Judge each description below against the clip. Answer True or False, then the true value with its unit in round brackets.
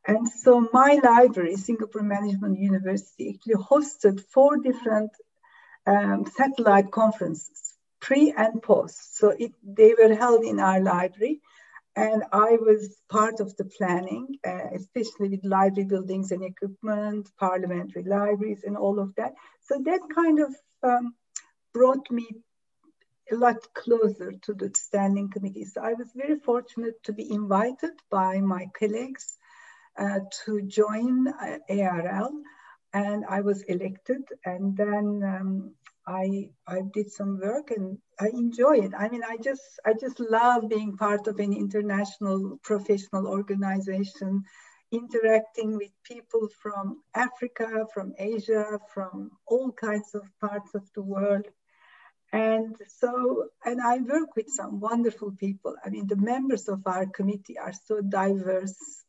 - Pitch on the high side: True (210 Hz)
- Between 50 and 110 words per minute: False (140 wpm)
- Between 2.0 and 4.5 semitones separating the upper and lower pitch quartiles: True (3.3 semitones)